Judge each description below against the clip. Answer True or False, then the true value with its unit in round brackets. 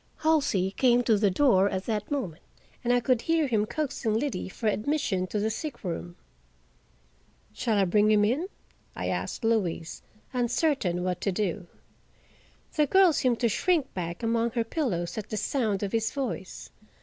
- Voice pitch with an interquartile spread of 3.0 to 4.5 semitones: False (5.2 semitones)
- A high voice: True (225 Hz)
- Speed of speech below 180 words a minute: True (170 wpm)